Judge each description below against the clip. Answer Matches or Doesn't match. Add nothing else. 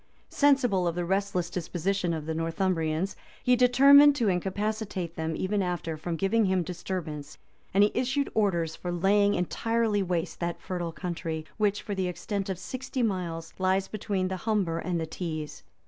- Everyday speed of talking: Matches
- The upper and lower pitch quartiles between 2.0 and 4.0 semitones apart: Matches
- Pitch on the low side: Doesn't match